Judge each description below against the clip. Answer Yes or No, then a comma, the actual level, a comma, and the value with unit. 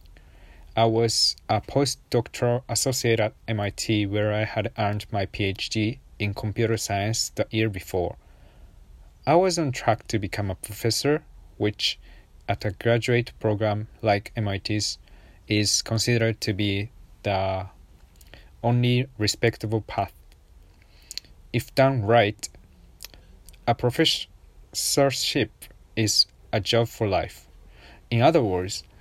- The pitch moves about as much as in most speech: Yes, average, 4.1 semitones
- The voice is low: Yes, low, 105 Hz